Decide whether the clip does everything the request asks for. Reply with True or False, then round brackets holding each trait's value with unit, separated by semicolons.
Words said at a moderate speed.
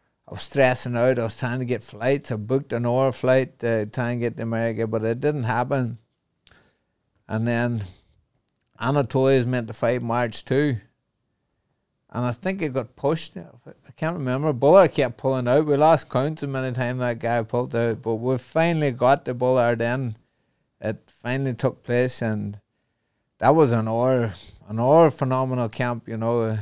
True (180 wpm)